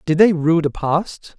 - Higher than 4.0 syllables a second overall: No, 3.9 syllables/s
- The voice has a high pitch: No, medium, 165 Hz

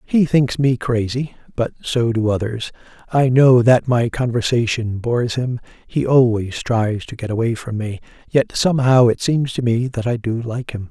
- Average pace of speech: Yes, average, 185 wpm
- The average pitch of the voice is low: Yes, low, 120 Hz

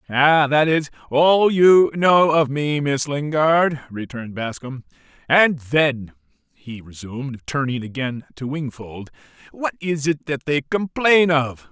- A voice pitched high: No, medium, 145 Hz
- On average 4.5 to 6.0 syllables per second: No, 3.9 syllables/s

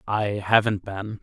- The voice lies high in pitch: No, low, 105 Hz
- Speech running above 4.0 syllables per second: No, 3.8 syllables/s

